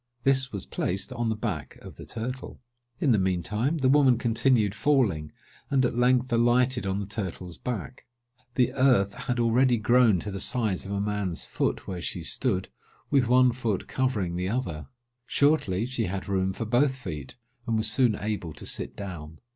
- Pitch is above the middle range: No, low, 110 Hz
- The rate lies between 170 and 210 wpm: Yes, average, 185 wpm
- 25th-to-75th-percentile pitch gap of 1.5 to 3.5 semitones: No, average, 4.9 semitones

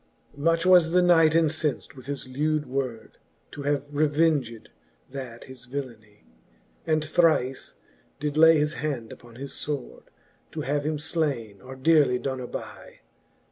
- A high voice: No, medium, 145 Hz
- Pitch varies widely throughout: No, average, 3.4 semitones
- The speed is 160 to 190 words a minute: No, average, 140 wpm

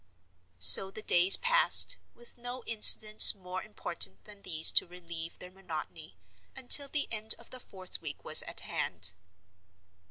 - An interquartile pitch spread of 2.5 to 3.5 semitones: No, average, 5.2 semitones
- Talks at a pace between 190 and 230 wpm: No, average, 150 wpm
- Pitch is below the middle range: No, high, 195 Hz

